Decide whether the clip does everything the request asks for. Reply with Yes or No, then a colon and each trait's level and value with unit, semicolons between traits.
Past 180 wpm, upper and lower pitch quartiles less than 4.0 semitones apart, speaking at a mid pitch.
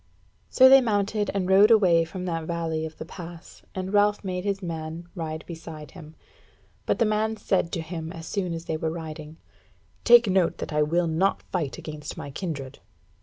Yes: average, 190 wpm; average, 3.6 semitones; medium, 170 Hz